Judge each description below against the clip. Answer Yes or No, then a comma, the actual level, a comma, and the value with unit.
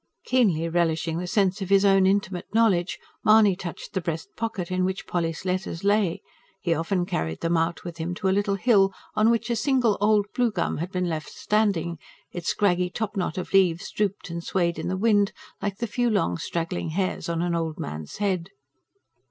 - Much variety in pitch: No, average, 3.3 semitones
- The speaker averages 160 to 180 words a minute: No, average, 200 wpm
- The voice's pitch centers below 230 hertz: Yes, medium, 185 Hz